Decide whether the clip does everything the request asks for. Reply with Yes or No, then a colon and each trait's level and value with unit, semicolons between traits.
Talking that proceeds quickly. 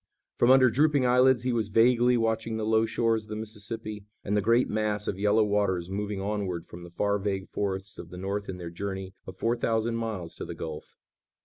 Yes: fast, 215 wpm